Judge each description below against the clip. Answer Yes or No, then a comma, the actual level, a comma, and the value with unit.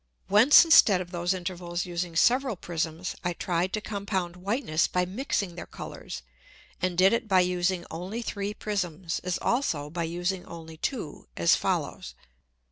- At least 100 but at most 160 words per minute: Yes, average, 155 wpm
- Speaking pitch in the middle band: Yes, medium, 180 Hz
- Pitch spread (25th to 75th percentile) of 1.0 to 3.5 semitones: Yes, average, 2.7 semitones